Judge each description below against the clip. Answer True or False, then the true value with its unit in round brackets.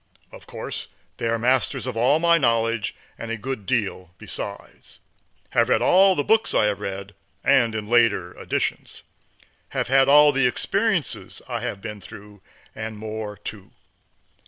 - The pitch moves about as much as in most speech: True (4.1 semitones)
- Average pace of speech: True (155 wpm)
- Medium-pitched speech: False (115 Hz)